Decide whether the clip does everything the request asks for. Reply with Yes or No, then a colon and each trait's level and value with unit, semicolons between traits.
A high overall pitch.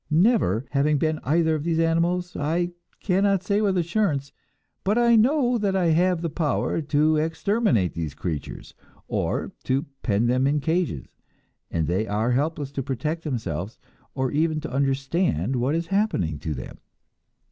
No: medium, 155 Hz